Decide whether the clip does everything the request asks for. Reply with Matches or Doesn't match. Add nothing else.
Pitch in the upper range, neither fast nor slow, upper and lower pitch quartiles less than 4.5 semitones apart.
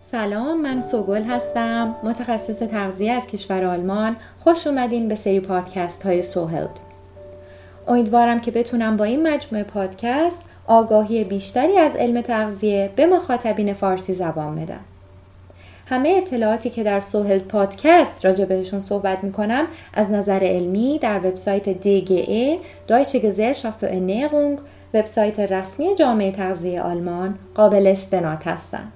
Matches